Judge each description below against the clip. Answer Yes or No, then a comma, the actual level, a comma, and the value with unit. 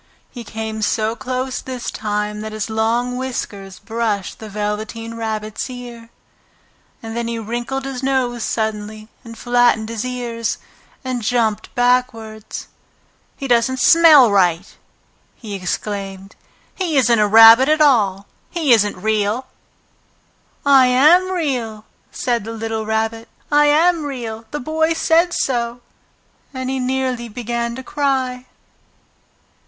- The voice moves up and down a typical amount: Yes, average, 3.0 semitones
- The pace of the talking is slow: Yes, slow, 130 wpm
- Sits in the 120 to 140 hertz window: No, high, 235 Hz